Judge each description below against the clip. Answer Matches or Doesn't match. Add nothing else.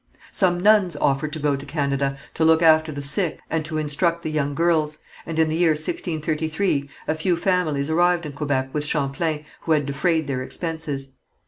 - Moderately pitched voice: Matches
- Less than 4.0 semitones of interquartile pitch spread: Matches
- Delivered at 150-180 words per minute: Doesn't match